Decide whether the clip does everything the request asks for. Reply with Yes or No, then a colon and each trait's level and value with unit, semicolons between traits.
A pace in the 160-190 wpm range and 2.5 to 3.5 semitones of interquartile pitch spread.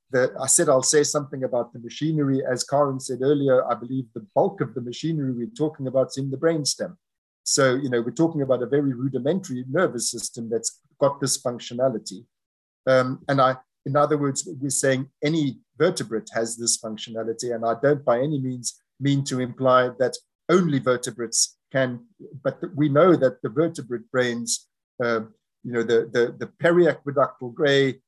Yes: average, 180 wpm; average, 3.1 semitones